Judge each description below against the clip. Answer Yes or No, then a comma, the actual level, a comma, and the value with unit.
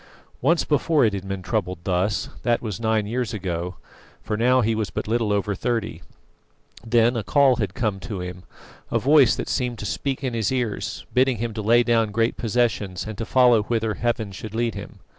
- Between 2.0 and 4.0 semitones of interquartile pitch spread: Yes, average, 2.9 semitones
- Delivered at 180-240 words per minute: Yes, average, 200 wpm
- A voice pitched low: Yes, low, 115 Hz